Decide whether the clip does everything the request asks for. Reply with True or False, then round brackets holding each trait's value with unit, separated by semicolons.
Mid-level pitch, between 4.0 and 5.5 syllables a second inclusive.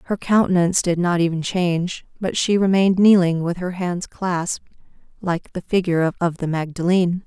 True (180 Hz; 5.4 syllables/s)